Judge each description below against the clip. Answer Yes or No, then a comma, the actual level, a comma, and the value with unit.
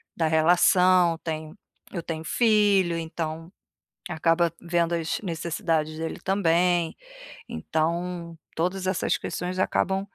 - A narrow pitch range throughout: Yes, narrow, 1.9 semitones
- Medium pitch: Yes, medium, 170 Hz